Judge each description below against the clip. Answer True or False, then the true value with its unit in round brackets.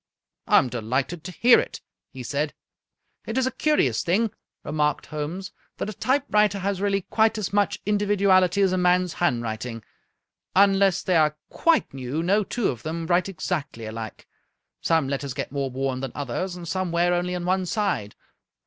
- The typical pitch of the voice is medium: True (175 Hz)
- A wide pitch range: True (6.0 semitones)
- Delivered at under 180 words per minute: False (185 wpm)